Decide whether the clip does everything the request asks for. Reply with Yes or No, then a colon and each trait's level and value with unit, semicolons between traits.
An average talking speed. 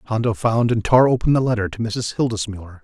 No: fast, 210 wpm